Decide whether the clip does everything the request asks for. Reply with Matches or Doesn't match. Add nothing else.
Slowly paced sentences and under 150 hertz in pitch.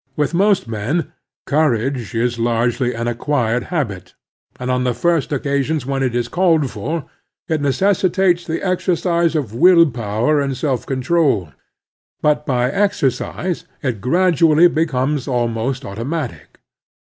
Matches